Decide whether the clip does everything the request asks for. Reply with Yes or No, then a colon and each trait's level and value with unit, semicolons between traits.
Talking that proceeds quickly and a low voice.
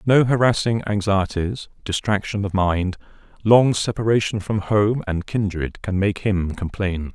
No: slow, 135 wpm; low, 100 Hz